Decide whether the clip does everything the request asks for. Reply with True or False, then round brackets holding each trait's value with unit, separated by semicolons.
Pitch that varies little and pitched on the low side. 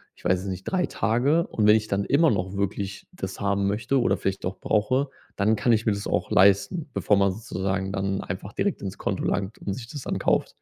False (3.1 semitones; 100 Hz)